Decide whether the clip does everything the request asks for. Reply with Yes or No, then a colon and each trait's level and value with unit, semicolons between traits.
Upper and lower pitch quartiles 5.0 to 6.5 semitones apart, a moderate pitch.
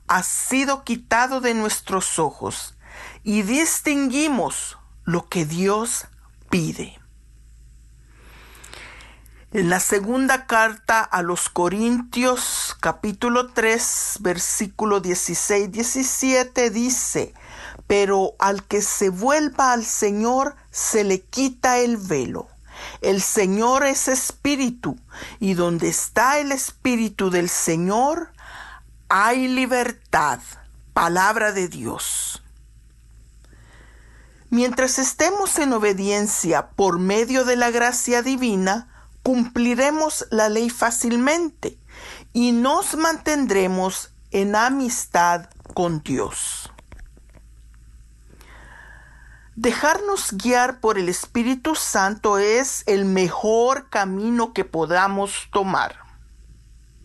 No: average, 5.3 semitones; high, 220 Hz